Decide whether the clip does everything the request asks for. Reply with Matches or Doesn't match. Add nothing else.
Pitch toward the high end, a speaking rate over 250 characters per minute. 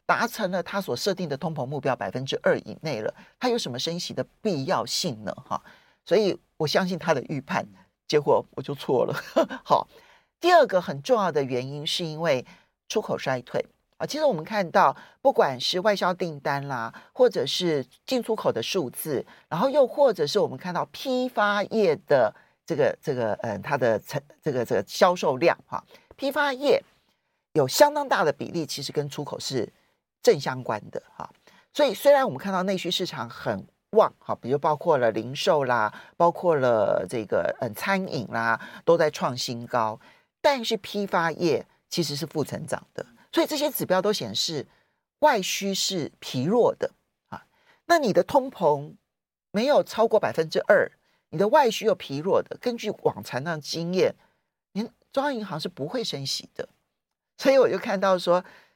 Matches